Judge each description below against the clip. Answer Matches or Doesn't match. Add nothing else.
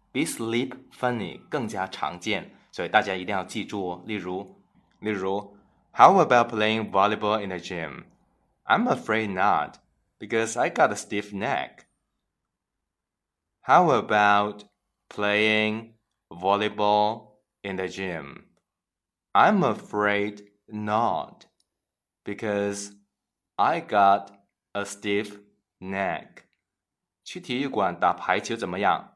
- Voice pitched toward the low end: Matches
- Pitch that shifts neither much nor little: Doesn't match